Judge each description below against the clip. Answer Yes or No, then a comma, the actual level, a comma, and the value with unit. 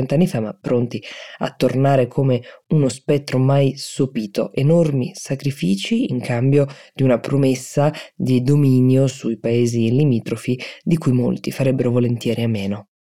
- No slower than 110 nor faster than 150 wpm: Yes, average, 135 wpm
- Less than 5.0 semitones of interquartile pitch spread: Yes, average, 2.8 semitones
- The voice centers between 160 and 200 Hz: No, low, 130 Hz